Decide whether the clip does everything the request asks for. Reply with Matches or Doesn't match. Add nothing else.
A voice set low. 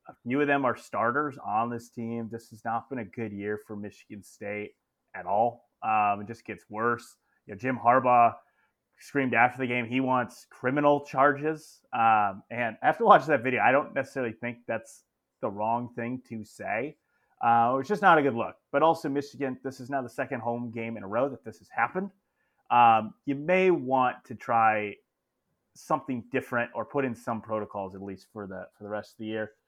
Matches